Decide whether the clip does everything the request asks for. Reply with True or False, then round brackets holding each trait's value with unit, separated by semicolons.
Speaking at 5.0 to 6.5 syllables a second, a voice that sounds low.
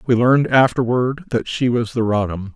True (5.1 syllables/s; 120 Hz)